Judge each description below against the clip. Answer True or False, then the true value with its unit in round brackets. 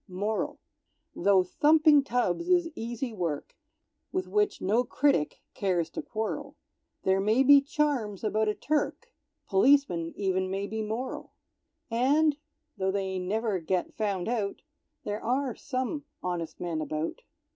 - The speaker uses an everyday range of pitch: False (6.6 semitones)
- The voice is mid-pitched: False (215 Hz)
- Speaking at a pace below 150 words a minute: True (135 wpm)